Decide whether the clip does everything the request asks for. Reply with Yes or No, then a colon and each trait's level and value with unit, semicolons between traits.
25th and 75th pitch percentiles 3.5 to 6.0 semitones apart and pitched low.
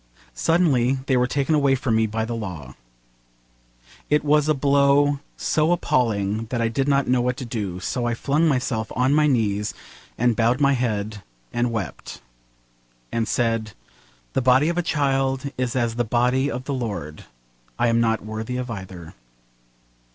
Yes: average, 3.8 semitones; low, 125 Hz